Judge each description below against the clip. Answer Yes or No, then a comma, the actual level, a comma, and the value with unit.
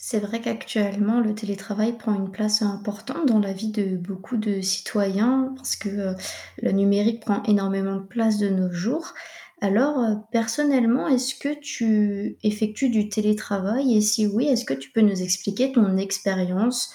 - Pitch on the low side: No, high, 210 Hz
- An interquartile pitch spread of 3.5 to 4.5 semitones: No, average, 2.8 semitones